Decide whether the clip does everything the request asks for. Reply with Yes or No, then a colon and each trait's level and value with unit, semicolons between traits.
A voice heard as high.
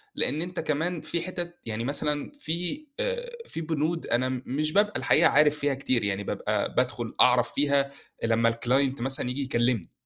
No: medium, 140 Hz